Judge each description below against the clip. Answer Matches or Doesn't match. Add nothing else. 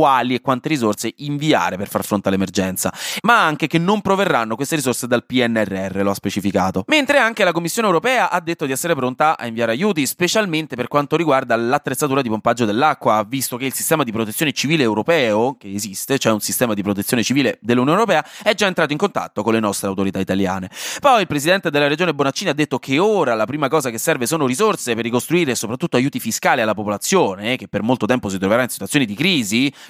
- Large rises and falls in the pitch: Matches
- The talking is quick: Matches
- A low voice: Matches